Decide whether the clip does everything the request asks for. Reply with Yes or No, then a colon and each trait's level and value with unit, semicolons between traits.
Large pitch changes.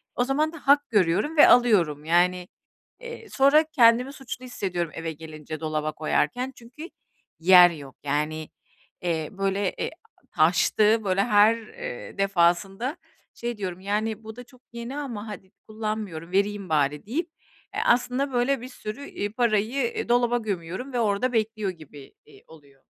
Yes: wide, 6.1 semitones